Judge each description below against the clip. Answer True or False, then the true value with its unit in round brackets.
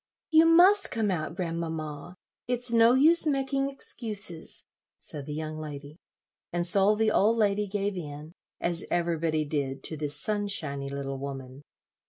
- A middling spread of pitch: False (6.7 semitones)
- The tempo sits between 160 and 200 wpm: False (145 wpm)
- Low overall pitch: False (175 Hz)